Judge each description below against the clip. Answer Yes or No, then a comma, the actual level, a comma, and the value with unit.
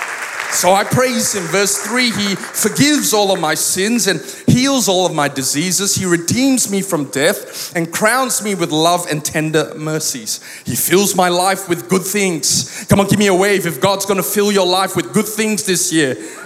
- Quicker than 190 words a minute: Yes, average, 200 wpm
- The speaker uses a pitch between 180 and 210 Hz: Yes, high, 190 Hz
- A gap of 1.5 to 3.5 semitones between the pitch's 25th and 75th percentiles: Yes, average, 3.1 semitones